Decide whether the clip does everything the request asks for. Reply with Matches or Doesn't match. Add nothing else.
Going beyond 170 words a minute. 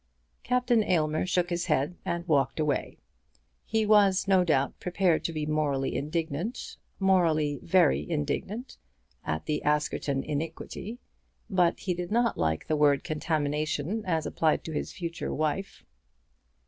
Doesn't match